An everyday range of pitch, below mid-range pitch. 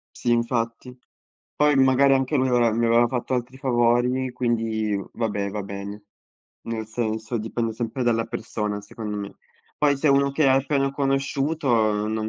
Yes: average, 3.2 semitones; low, 120 Hz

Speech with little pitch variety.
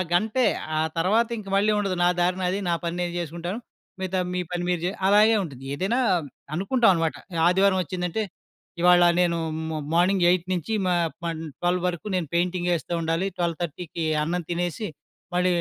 Yes: narrow, 1.9 semitones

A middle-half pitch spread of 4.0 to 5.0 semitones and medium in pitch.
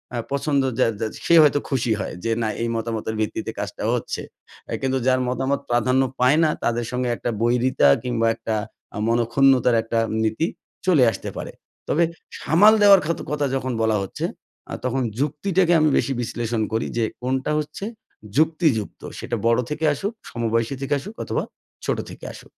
No: average, 4.3 semitones; low, 130 Hz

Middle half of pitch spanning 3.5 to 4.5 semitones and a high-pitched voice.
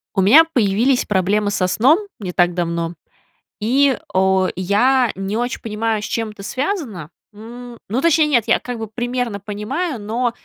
Yes: average, 4.2 semitones; high, 225 Hz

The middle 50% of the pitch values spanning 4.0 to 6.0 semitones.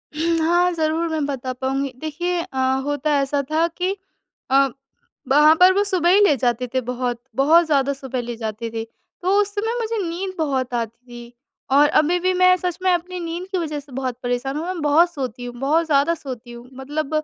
Yes: average, 5.0 semitones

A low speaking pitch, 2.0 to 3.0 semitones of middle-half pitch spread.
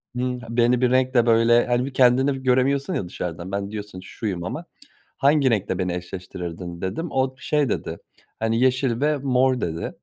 No: low, 120 Hz; wide, 5.6 semitones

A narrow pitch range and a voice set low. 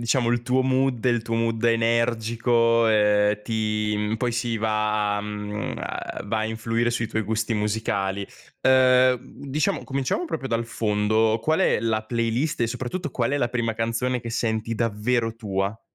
Yes: narrow, 1.9 semitones; low, 115 Hz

